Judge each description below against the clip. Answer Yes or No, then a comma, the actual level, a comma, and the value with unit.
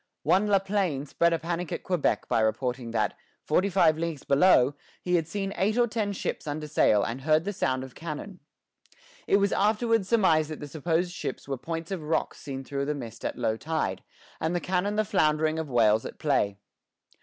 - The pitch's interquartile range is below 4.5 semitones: No, wide, 5.5 semitones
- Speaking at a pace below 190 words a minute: No, average, 200 wpm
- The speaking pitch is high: No, medium, 160 Hz